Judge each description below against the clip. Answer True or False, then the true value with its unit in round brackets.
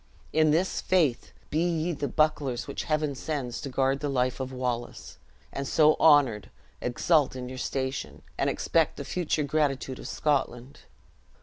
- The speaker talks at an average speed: True (160 wpm)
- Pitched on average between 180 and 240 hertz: False (140 Hz)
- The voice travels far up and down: False (3.1 semitones)